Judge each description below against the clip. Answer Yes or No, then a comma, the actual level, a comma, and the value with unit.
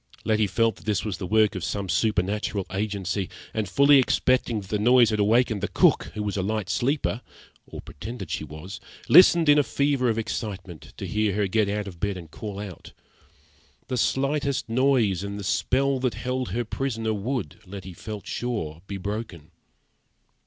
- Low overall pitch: Yes, low, 105 Hz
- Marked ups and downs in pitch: No, average, 4.0 semitones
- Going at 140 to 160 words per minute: No, average, 180 wpm